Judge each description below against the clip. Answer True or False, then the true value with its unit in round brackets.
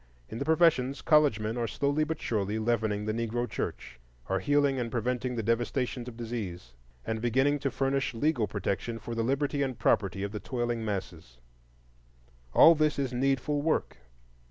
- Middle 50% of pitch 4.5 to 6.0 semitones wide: False (4.1 semitones)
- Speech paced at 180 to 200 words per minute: False (170 wpm)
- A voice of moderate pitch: False (120 Hz)